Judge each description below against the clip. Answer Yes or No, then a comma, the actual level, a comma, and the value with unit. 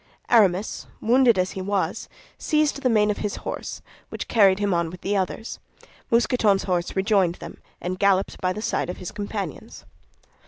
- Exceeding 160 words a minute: Yes, average, 170 wpm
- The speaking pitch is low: No, high, 200 Hz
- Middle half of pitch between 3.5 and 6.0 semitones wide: No, average, 3.0 semitones